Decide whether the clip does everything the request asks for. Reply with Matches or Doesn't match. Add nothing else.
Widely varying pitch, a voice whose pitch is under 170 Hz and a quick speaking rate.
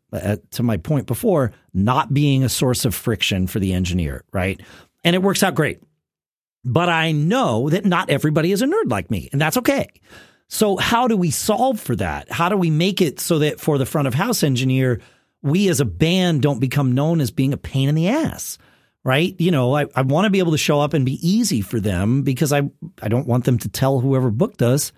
Matches